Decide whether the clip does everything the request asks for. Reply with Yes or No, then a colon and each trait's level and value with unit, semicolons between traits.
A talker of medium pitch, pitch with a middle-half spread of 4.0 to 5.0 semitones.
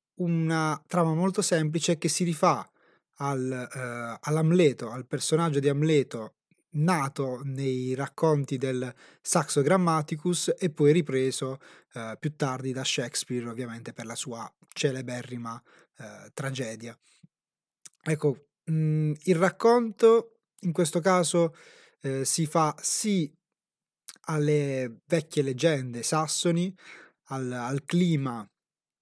Yes: medium, 150 Hz; average, 4.6 semitones